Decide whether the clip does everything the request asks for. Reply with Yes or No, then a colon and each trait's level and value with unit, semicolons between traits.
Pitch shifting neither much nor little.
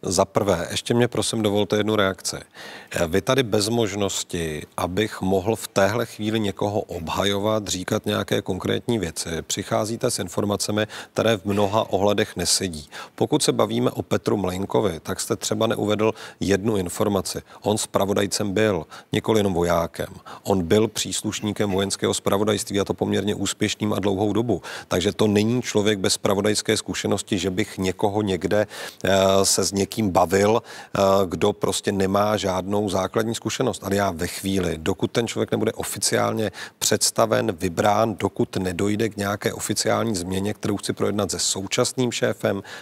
No: narrow, 2.0 semitones